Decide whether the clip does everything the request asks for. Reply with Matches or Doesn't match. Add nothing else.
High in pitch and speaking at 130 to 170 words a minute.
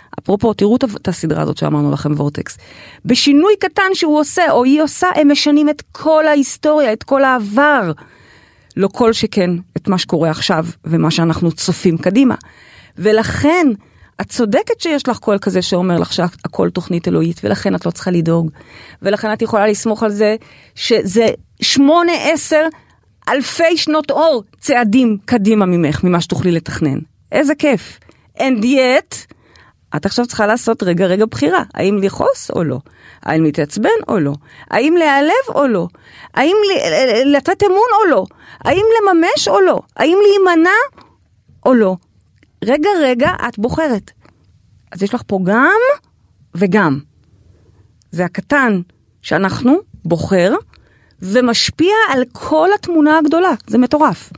Matches